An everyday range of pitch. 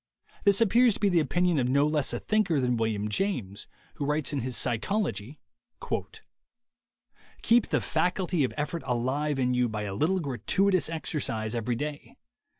No: wide, 6.6 semitones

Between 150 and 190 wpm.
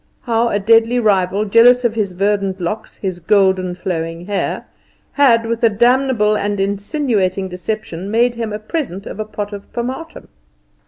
Yes: average, 160 wpm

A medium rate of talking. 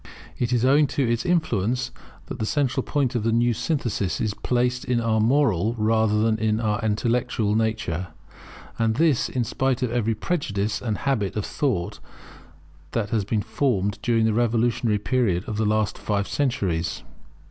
Yes: average, 165 wpm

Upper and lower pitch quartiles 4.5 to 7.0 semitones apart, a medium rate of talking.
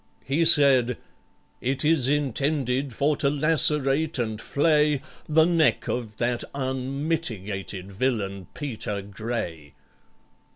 No: average, 5.2 semitones; slow, 100 wpm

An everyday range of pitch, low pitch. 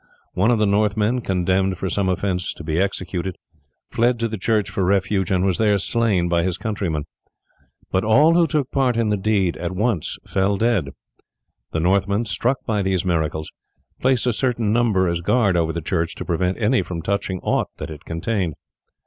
Yes: average, 3.9 semitones; low, 100 Hz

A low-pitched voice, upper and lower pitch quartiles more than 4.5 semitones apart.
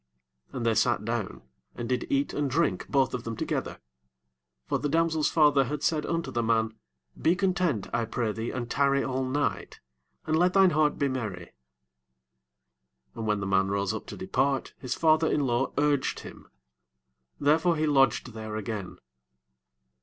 Yes: low, 130 Hz; average, 5.0 semitones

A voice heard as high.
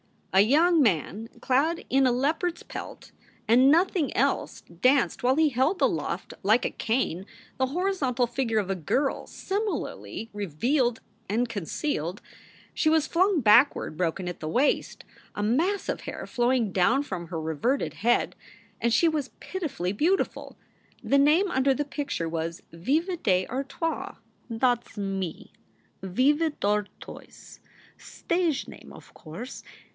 Yes: very high, 255 Hz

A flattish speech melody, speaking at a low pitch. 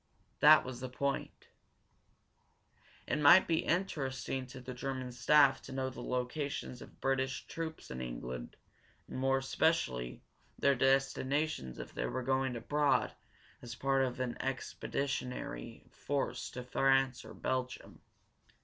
Yes: narrow, 1.8 semitones; low, 130 Hz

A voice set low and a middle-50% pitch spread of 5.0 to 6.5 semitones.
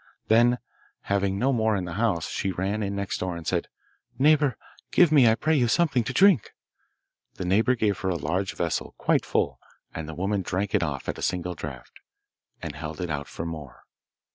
Yes: low, 100 Hz; wide, 5.5 semitones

